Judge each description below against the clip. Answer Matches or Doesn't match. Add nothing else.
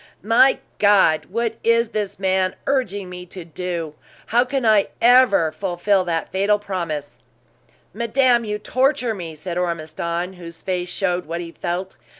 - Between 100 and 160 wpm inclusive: Matches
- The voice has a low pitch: Doesn't match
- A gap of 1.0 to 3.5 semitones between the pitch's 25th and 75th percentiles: Doesn't match